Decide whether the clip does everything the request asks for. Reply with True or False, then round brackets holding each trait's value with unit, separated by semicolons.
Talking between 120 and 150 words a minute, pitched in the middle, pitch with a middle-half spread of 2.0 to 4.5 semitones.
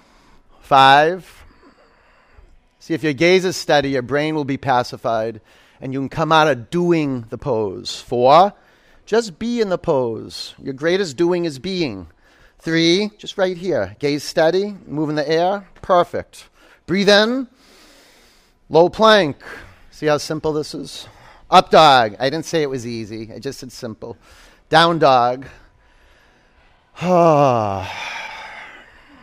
False (135 wpm; 155 Hz; 5.1 semitones)